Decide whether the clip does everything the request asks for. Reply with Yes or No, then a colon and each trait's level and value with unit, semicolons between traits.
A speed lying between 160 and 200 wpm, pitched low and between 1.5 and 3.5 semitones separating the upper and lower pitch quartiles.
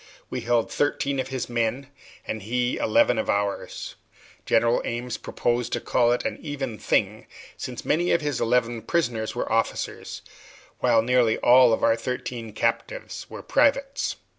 No: average, 150 wpm; low, 120 Hz; average, 2.7 semitones